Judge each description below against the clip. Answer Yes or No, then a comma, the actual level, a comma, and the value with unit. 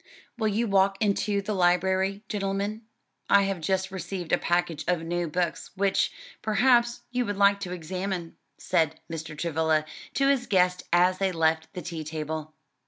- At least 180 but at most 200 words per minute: No, average, 165 wpm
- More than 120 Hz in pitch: Yes, medium, 185 Hz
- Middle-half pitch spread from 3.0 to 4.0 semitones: Yes, average, 3.3 semitones